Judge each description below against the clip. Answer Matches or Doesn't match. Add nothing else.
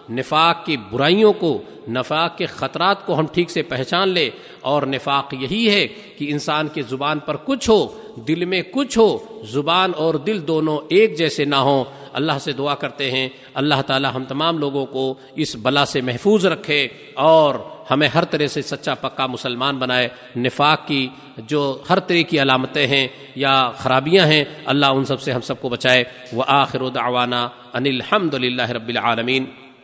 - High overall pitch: Doesn't match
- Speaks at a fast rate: Doesn't match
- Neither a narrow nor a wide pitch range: Matches